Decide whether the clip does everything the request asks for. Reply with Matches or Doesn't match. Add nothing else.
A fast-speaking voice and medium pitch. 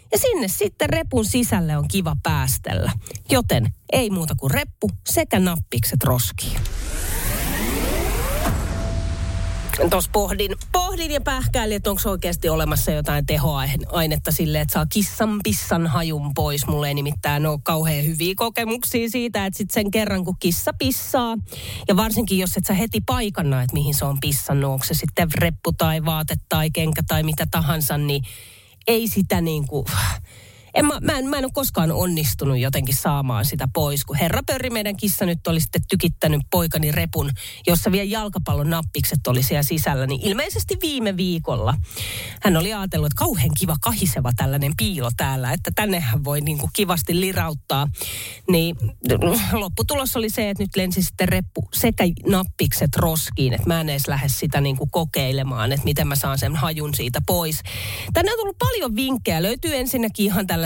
Matches